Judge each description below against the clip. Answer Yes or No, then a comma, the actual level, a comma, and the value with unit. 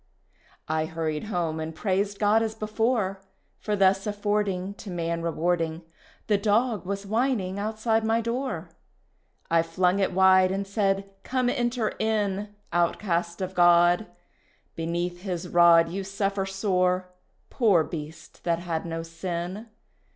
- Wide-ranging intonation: No, average, 3.5 semitones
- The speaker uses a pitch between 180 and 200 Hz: Yes, high, 190 Hz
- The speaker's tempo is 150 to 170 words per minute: No, slow, 135 wpm